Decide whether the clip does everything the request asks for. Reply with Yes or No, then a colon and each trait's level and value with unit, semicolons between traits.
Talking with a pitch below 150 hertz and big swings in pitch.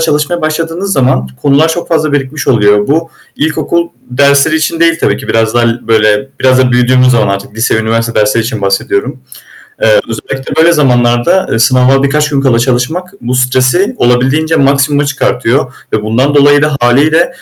No: low, 135 Hz; average, 4.4 semitones